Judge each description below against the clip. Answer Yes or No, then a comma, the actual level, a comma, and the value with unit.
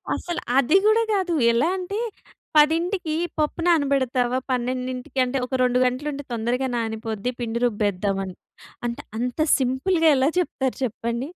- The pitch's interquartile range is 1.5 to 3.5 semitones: No, average, 4.5 semitones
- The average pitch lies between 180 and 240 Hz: No, very high, 255 Hz